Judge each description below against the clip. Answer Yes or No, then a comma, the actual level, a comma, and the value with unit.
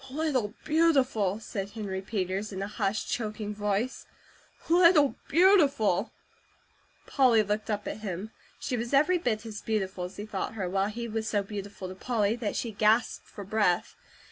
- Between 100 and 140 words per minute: No, average, 165 wpm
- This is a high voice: Yes, high, 215 Hz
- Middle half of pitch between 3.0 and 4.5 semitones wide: Yes, average, 3.4 semitones